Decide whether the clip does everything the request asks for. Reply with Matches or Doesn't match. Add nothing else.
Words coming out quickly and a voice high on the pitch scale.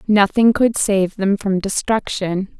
Doesn't match